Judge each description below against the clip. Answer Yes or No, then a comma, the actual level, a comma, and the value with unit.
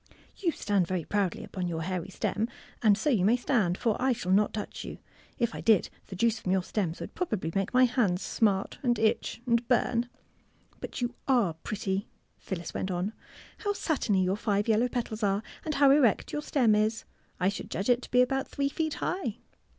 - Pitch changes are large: No, average, 4.4 semitones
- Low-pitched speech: No, high, 215 Hz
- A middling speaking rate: No, fast, 210 wpm